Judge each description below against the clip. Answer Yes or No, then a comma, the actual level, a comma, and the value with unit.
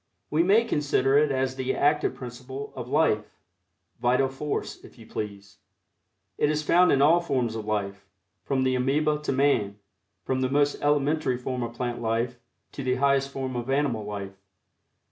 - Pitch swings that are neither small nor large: Yes, average, 3.2 semitones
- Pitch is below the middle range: Yes, low, 130 Hz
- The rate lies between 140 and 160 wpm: No, average, 170 wpm